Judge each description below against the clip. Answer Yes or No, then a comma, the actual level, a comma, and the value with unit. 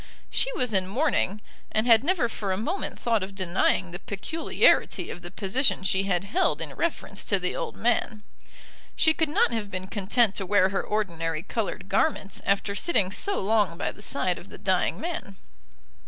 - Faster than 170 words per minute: Yes, average, 185 wpm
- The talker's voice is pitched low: No, high, 205 Hz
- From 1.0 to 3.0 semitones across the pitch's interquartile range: No, average, 4.3 semitones